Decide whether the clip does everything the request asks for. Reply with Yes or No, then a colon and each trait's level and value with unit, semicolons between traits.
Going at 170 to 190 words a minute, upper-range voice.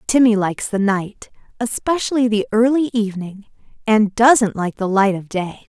No: average, 155 wpm; high, 215 Hz